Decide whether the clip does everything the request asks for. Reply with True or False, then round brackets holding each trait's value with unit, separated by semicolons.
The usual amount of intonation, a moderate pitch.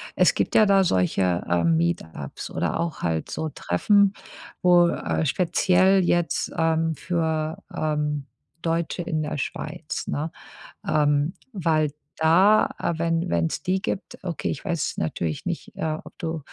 True (3.4 semitones; 160 Hz)